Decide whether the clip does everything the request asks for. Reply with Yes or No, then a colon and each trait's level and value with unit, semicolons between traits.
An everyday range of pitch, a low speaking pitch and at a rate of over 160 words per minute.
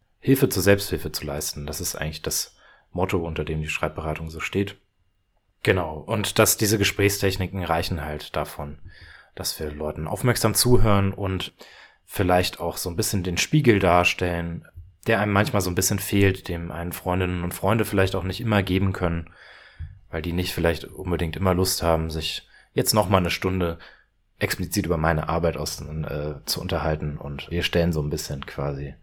Yes: average, 3.4 semitones; very low, 90 Hz; average, 175 wpm